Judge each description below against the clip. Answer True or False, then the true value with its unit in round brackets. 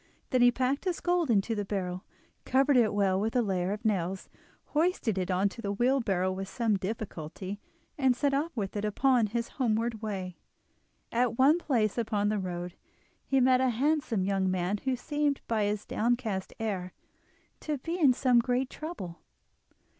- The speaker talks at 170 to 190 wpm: True (175 wpm)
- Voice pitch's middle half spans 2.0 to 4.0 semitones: False (4.9 semitones)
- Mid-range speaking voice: False (225 Hz)